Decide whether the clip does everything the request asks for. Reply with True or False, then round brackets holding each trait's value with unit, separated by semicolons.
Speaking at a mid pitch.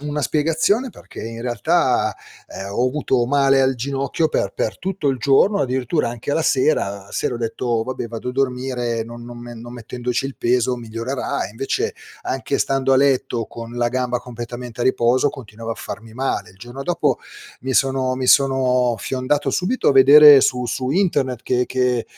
False (125 Hz)